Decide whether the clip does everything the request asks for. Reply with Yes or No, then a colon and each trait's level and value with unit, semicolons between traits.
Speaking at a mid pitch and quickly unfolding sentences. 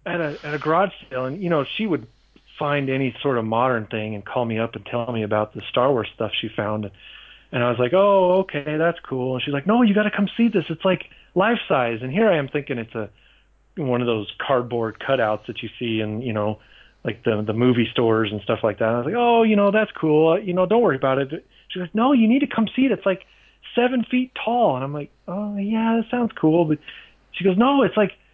Yes: medium, 145 Hz; fast, 260 wpm